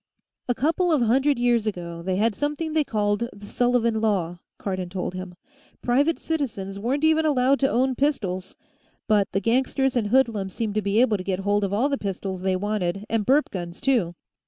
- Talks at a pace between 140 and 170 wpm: No, average, 195 wpm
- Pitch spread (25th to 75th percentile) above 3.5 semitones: Yes, wide, 5.5 semitones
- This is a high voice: Yes, high, 220 Hz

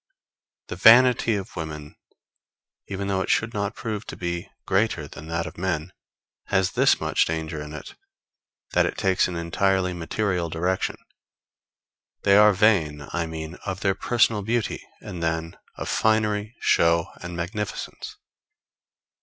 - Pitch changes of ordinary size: Yes, average, 3.9 semitones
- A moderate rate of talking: Yes, average, 145 wpm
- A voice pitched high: No, very low, 95 Hz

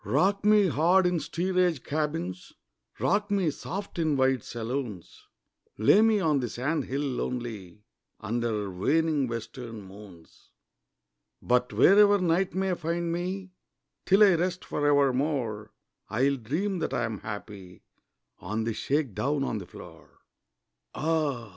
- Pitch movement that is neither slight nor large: No, wide, 7.6 semitones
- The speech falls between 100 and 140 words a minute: Yes, slow, 135 wpm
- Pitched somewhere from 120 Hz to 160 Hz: Yes, medium, 140 Hz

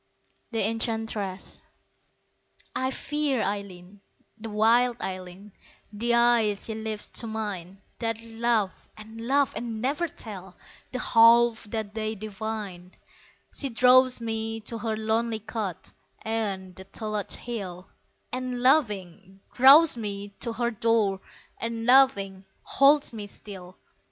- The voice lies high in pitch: Yes, high, 220 Hz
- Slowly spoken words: Yes, slow, 120 wpm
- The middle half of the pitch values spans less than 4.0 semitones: Yes, average, 2.9 semitones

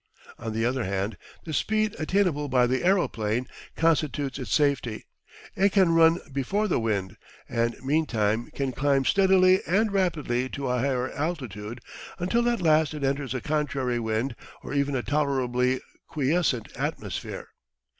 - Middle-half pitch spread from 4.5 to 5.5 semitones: Yes, average, 5.1 semitones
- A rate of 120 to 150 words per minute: Yes, average, 145 wpm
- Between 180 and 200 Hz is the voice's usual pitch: No, medium, 140 Hz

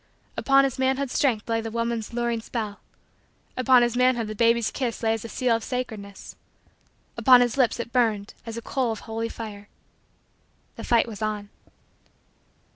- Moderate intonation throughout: No, narrow, 2.1 semitones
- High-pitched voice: Yes, high, 230 Hz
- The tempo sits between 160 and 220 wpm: Yes, average, 170 wpm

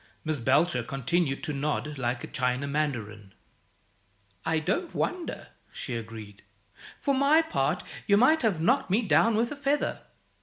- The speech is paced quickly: No, average, 150 wpm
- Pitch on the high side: No, medium, 155 Hz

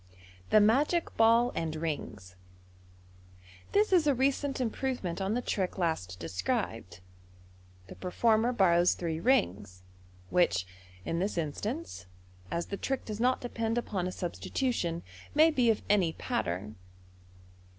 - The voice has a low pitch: No, high, 190 Hz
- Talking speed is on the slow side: Yes, slow, 130 wpm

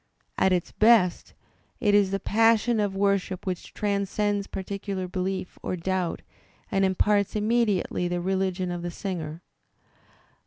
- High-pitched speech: Yes, high, 195 Hz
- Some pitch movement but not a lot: No, narrow, 2.1 semitones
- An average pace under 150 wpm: Yes, average, 140 wpm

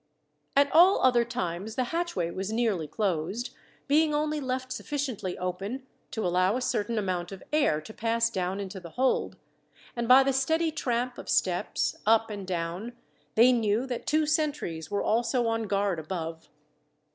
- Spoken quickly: No, average, 165 wpm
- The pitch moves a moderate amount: No, wide, 5.7 semitones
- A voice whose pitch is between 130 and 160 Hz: No, high, 225 Hz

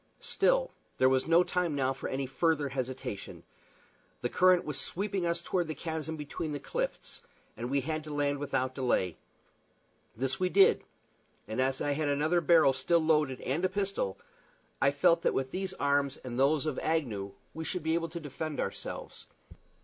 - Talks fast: No, average, 180 wpm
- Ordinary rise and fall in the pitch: Yes, average, 4.1 semitones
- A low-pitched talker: No, medium, 150 Hz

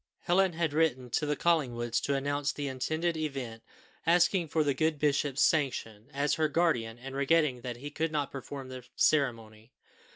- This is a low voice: No, medium, 145 Hz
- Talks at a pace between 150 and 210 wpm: Yes, average, 170 wpm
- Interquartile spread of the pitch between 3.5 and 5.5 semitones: Yes, average, 3.8 semitones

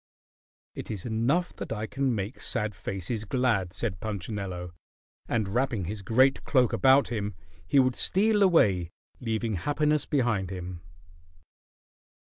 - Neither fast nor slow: No, slow, 130 wpm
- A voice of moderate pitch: No, low, 110 Hz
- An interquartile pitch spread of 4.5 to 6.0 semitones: Yes, average, 5.1 semitones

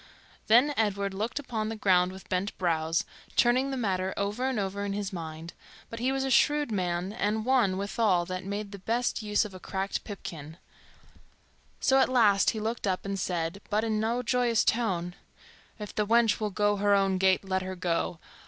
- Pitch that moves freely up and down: No, average, 3.5 semitones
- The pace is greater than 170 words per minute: Yes, average, 195 wpm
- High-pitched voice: Yes, high, 205 Hz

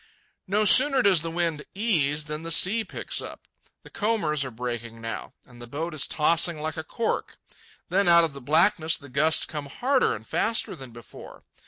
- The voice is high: No, medium, 160 Hz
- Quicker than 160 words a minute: Yes, average, 190 wpm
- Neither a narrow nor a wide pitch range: No, wide, 5.7 semitones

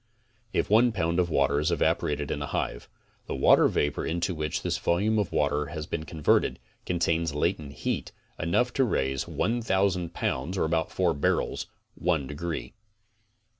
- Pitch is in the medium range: No, very low, 85 Hz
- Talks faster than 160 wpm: No, average, 155 wpm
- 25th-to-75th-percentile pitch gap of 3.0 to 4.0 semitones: Yes, average, 3.7 semitones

